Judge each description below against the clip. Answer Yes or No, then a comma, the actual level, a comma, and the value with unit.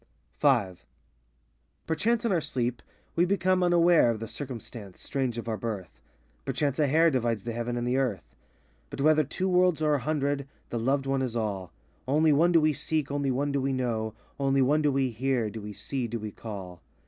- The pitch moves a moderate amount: Yes, average, 4.8 semitones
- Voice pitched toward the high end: No, low, 135 Hz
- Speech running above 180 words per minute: Yes, average, 200 wpm